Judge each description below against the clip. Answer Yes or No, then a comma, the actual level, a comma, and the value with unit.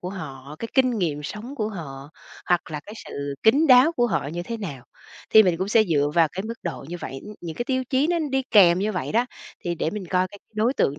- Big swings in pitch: Yes, wide, 6.3 semitones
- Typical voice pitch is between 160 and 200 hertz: Yes, high, 190 Hz